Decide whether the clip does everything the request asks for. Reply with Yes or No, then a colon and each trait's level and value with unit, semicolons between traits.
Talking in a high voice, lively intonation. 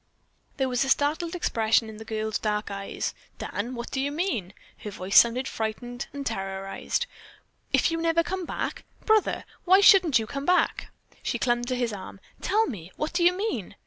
Yes: very high, 250 Hz; wide, 7.4 semitones